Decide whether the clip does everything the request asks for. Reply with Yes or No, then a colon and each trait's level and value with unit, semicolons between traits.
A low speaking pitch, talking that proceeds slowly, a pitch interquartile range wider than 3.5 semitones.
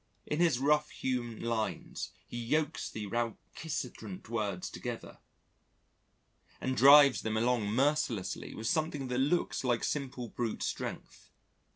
Yes: low, 125 Hz; slow, 120 wpm; average, 4.3 semitones